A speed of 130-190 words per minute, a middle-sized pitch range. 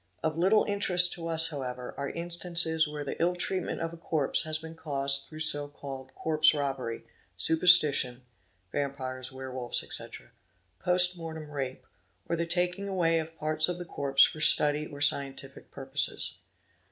Yes: average, 155 wpm; average, 3.4 semitones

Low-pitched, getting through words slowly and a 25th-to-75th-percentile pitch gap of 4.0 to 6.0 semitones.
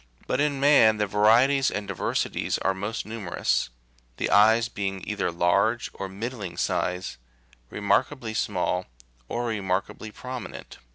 No: low, 105 Hz; slow, 130 wpm; average, 3.5 semitones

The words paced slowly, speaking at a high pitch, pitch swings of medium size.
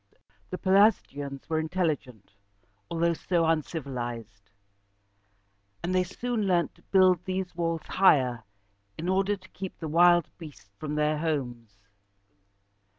No: slow, 125 wpm; medium, 165 Hz; average, 5.0 semitones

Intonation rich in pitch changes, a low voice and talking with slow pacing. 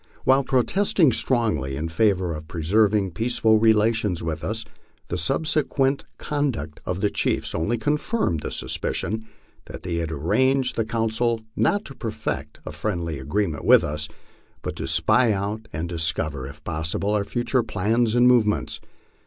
No: wide, 6.4 semitones; low, 105 Hz; average, 155 wpm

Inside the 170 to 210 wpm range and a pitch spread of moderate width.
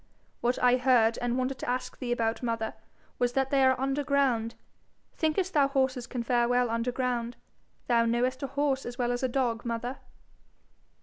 No: average, 185 wpm; narrow, 2.0 semitones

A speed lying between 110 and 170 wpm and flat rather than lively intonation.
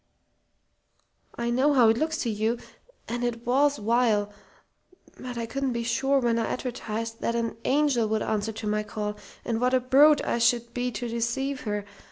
No: average, 185 wpm; narrow, 2.3 semitones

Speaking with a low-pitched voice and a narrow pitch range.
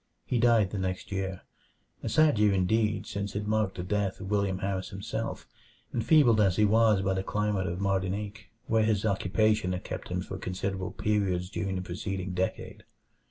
Yes: low, 100 Hz; narrow, 2.2 semitones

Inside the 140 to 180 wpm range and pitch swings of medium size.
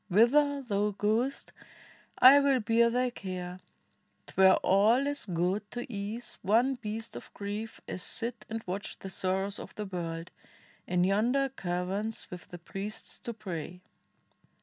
Yes: average, 150 wpm; average, 4.2 semitones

